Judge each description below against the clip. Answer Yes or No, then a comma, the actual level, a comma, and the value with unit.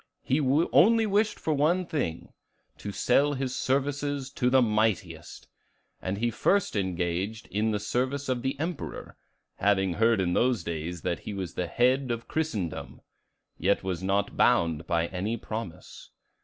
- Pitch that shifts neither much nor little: No, wide, 6.7 semitones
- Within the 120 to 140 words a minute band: No, average, 155 wpm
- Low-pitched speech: Yes, low, 110 Hz